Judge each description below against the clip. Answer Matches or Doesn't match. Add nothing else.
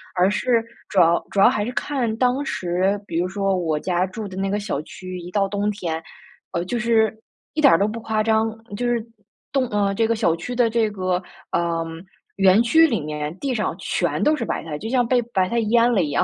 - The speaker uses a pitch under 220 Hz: Matches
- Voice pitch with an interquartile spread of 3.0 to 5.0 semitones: Matches